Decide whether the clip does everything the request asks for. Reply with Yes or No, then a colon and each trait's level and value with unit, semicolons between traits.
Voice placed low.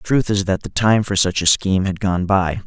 Yes: very low, 95 Hz